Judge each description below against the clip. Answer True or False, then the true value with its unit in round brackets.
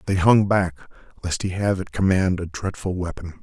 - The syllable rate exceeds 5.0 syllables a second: True (5.2 syllables/s)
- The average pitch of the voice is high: False (95 Hz)